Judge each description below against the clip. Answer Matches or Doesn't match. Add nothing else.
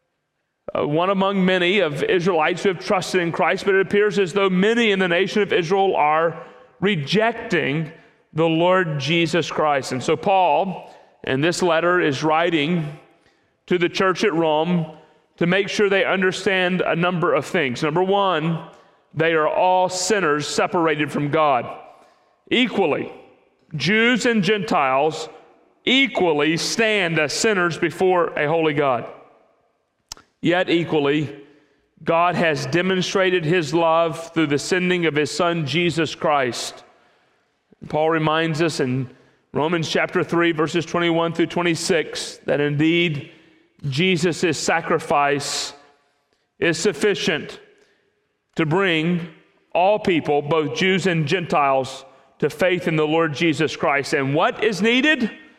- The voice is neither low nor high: Matches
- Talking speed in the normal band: Doesn't match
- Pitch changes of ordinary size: Matches